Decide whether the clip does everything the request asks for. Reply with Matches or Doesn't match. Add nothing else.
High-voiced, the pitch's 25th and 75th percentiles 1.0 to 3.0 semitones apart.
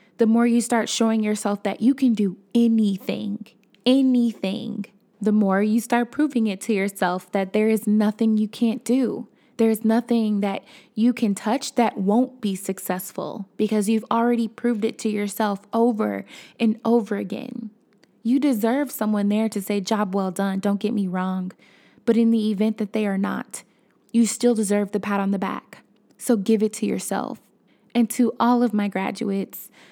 Matches